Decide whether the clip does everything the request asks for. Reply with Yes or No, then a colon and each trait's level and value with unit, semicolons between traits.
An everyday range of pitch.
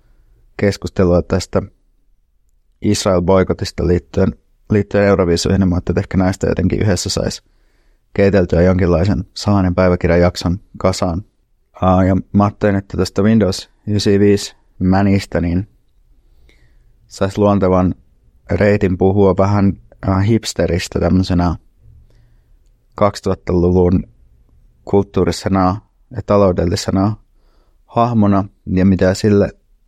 No: narrow, 2.3 semitones